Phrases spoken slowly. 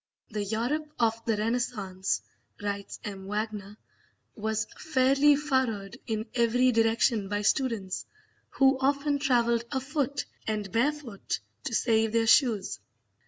Yes: slow, 120 wpm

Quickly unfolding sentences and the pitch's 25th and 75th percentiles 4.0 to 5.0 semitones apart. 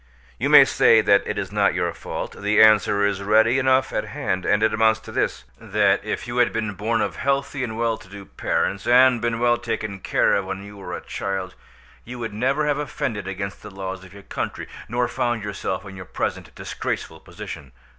No: fast, 210 wpm; average, 3.2 semitones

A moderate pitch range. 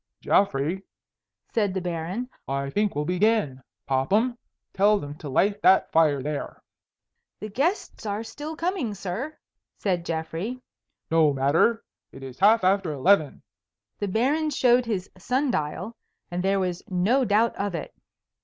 No: wide, 6.0 semitones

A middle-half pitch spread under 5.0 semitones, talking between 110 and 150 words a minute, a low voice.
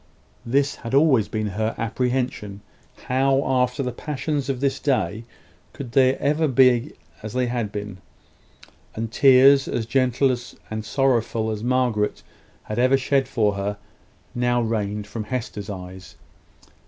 Yes: average, 3.6 semitones; average, 140 wpm; low, 125 Hz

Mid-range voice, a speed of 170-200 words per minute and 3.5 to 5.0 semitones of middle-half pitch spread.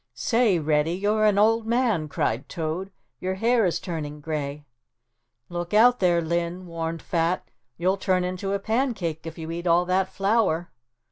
No: medium, 180 Hz; average, 160 wpm; average, 3.8 semitones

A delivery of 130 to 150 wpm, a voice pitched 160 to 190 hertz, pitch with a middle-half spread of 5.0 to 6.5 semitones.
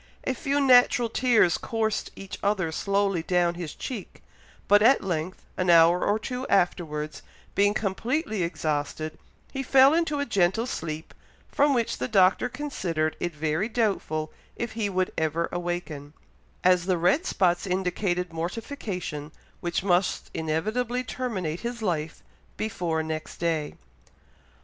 Yes: slow, 135 wpm; medium, 185 Hz; wide, 5.6 semitones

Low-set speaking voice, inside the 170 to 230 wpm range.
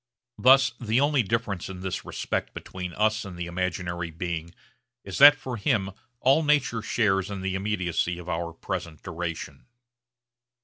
No: very low, 95 Hz; average, 150 wpm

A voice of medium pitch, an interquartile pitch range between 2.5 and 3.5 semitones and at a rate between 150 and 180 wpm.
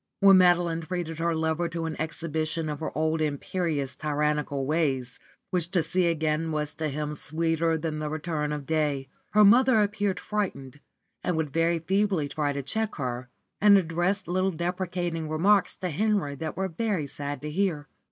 Yes: medium, 160 Hz; average, 3.2 semitones; average, 170 wpm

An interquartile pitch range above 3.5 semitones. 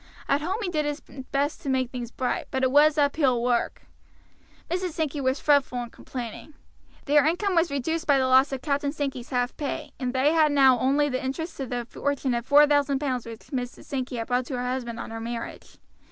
No: average, 2.9 semitones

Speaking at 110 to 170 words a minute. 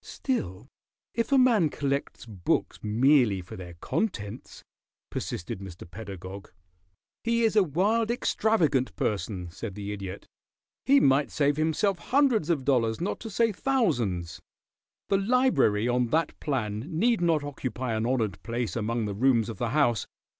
Yes: average, 150 wpm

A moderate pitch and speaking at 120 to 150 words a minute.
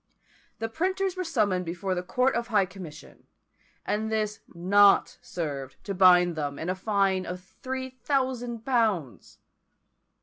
No: high, 200 Hz; average, 140 wpm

